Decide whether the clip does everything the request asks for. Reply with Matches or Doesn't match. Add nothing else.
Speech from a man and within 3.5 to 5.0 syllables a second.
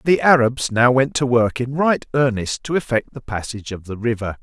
Doesn't match